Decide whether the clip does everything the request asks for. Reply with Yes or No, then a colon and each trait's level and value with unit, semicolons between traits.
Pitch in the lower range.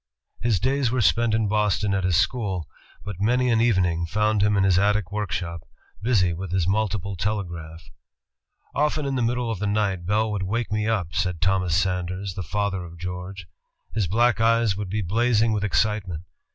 Yes: low, 100 Hz